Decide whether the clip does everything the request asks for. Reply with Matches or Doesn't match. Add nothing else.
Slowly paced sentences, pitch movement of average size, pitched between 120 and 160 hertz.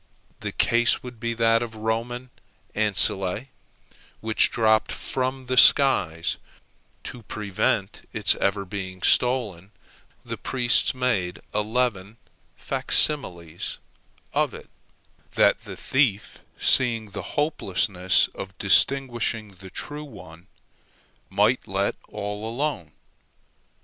Doesn't match